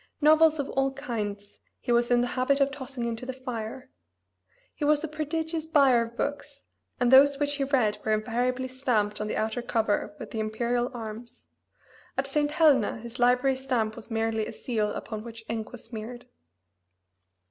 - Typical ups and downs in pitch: Yes, average, 3.6 semitones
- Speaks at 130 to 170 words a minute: No, average, 180 wpm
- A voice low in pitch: No, high, 245 Hz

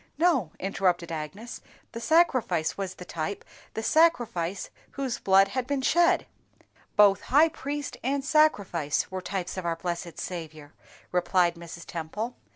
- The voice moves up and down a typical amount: No, wide, 7.6 semitones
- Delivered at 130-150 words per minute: Yes, average, 140 wpm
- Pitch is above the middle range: Yes, high, 195 Hz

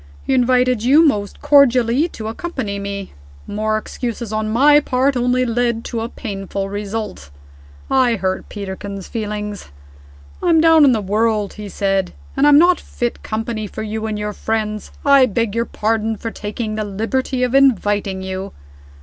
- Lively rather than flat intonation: No, average, 3.5 semitones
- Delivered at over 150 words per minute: Yes, average, 160 wpm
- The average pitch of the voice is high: Yes, high, 220 Hz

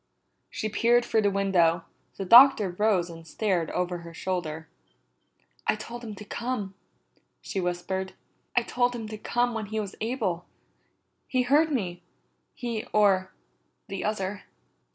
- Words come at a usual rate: Yes, average, 145 wpm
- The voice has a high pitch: Yes, high, 205 Hz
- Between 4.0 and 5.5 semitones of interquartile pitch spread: Yes, average, 4.4 semitones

